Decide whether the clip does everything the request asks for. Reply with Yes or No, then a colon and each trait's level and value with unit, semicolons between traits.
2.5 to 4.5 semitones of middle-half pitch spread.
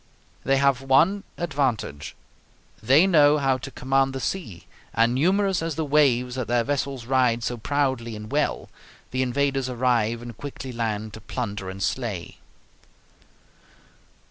Yes: average, 3.4 semitones